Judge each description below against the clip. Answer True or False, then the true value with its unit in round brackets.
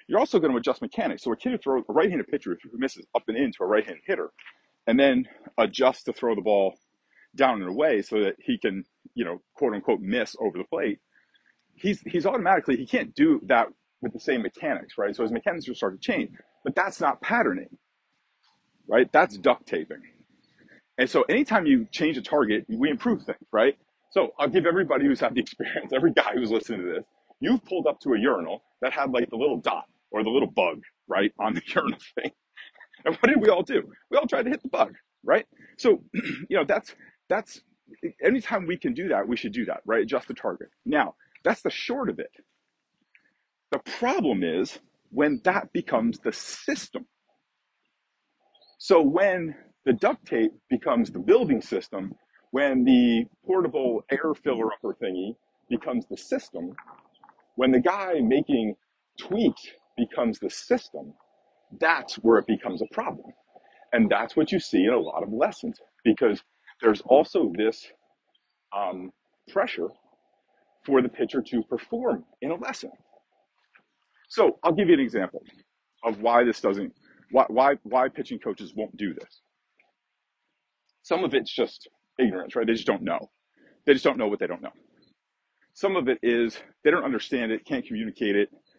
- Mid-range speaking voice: False (235 Hz)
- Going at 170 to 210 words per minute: True (180 wpm)